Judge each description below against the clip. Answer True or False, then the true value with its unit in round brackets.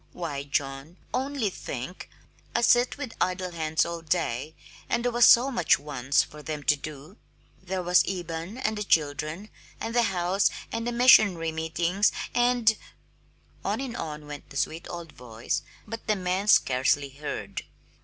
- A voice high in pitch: False (175 Hz)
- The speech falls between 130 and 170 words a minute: True (165 wpm)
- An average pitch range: False (6.4 semitones)